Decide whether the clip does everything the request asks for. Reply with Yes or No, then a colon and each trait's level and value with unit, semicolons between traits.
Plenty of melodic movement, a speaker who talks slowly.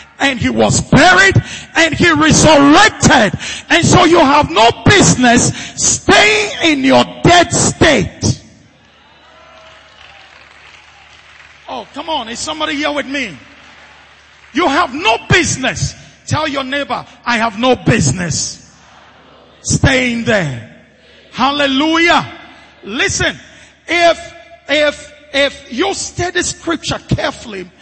No: average, 4.3 semitones; slow, 105 wpm